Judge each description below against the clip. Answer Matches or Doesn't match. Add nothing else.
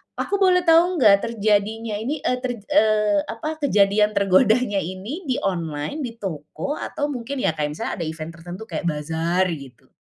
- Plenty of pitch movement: Matches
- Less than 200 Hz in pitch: Doesn't match